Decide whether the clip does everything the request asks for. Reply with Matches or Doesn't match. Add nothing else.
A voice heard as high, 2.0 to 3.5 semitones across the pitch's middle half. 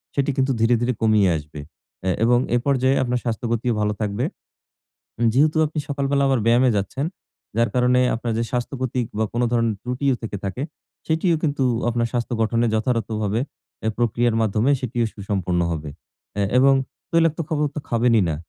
Doesn't match